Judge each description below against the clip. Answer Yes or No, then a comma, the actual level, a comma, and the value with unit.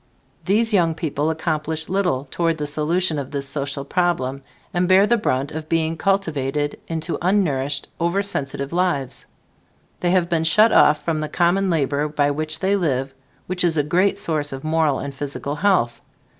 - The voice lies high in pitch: No, medium, 160 Hz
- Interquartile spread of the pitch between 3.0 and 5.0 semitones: Yes, average, 3.8 semitones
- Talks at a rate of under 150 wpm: No, average, 170 wpm